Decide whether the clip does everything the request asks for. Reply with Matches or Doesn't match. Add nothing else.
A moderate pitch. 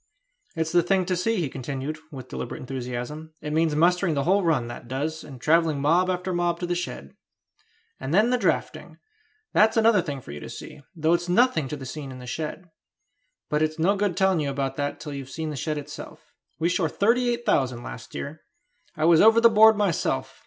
Matches